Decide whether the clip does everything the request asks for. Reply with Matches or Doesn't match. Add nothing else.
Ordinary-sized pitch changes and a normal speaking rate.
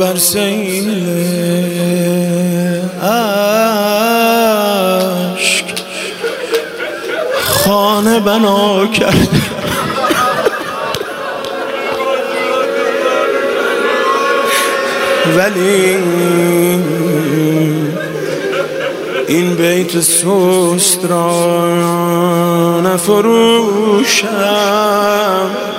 Doesn't match